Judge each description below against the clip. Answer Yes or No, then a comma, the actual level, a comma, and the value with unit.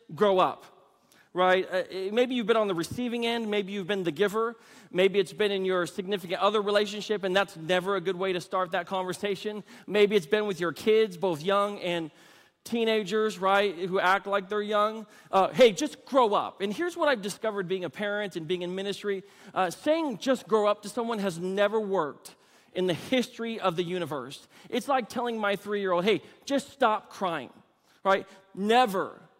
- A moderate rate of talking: Yes, average, 195 wpm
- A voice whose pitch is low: No, high, 200 Hz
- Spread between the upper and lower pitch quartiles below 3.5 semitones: Yes, average, 2.7 semitones